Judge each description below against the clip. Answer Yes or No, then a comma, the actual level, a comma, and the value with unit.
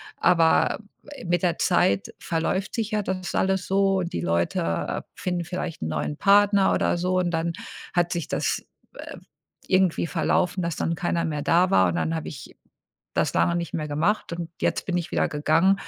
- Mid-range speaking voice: Yes, medium, 175 Hz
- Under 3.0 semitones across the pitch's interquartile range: Yes, narrow, 2.5 semitones